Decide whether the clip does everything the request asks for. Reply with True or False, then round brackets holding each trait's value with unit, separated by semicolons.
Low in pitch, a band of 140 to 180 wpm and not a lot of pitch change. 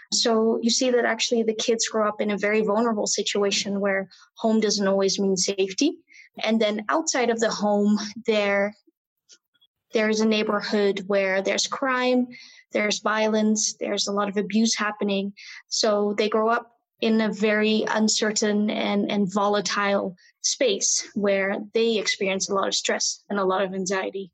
False (215 Hz; 160 wpm; 1.9 semitones)